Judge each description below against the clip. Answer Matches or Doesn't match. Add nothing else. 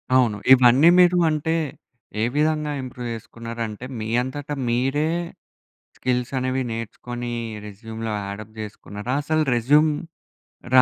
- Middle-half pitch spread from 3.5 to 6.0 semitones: Matches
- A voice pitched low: Matches